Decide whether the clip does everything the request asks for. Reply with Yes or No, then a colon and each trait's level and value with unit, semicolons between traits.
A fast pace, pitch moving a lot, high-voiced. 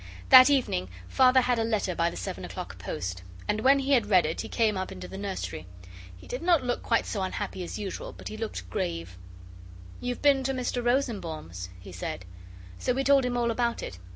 Yes: fast, 210 wpm; wide, 7.1 semitones; high, 225 Hz